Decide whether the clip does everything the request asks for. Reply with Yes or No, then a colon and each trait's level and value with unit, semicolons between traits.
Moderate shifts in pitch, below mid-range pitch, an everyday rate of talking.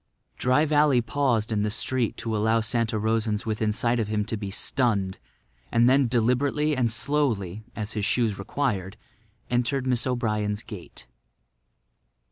Yes: average, 3.0 semitones; low, 115 Hz; average, 145 wpm